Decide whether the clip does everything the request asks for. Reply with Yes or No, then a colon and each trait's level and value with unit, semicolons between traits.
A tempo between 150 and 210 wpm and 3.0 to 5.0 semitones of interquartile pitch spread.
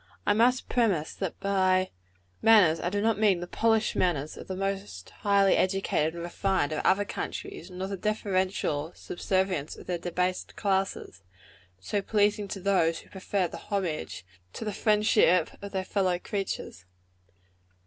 No: average, 155 wpm; narrow, 2.6 semitones